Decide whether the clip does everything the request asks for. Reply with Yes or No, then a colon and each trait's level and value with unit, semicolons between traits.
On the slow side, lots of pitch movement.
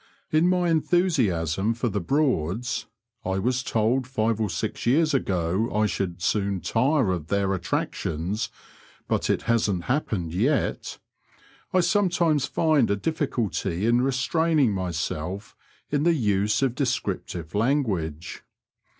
Yes: slow, 125 wpm; wide, 7.0 semitones